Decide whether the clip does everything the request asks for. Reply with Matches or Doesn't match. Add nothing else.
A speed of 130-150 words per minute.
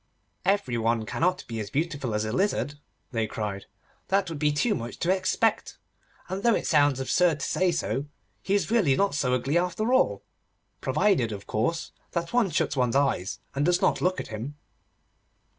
Doesn't match